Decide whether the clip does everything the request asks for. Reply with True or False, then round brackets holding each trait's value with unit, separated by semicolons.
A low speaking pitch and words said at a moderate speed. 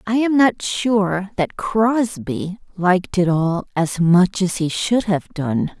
False (190 Hz; 165 wpm)